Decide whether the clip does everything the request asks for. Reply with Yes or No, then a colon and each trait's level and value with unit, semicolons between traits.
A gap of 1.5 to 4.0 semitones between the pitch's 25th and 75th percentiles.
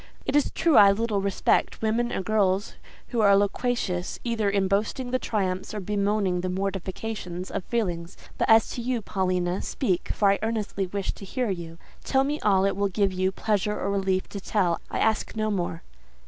Yes: average, 2.8 semitones